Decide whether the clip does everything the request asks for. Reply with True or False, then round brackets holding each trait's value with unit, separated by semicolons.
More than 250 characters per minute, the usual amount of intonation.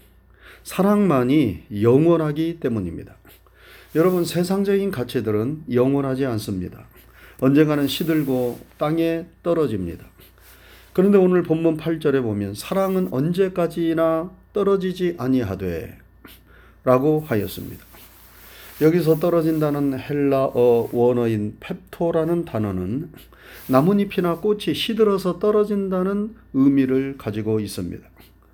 False (265 characters per minute; 7.0 semitones)